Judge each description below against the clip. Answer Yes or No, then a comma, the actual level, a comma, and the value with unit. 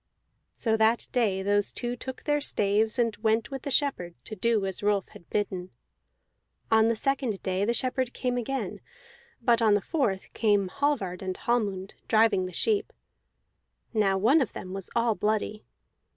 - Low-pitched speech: No, high, 220 Hz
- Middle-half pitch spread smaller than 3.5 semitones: No, average, 3.9 semitones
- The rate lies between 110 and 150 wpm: No, average, 165 wpm